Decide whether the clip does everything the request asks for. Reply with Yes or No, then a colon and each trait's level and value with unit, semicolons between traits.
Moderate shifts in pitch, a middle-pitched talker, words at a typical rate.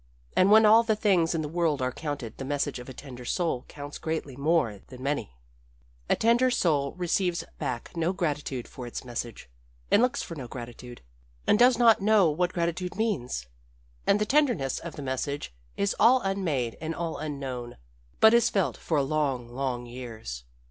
No: wide, 7.1 semitones; medium, 150 Hz; average, 180 wpm